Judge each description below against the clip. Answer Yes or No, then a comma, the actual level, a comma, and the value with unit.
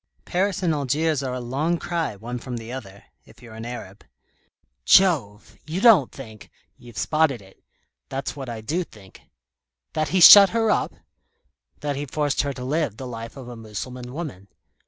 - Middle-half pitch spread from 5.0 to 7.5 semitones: Yes, wide, 5.5 semitones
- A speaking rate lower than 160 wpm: No, average, 180 wpm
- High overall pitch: No, low, 130 Hz